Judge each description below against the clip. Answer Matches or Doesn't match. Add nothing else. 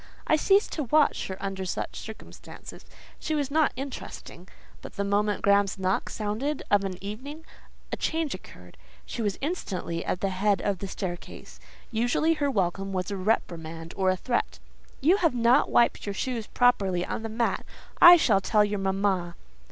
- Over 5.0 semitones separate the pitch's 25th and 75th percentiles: Matches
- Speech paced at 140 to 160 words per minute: Doesn't match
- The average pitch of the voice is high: Matches